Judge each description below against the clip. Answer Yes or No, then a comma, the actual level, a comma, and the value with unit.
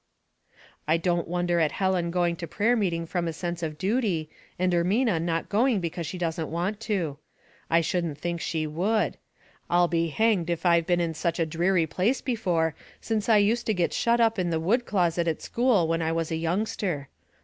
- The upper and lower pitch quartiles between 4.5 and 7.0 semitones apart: No, average, 3.5 semitones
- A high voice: No, medium, 175 Hz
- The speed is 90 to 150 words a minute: No, fast, 205 wpm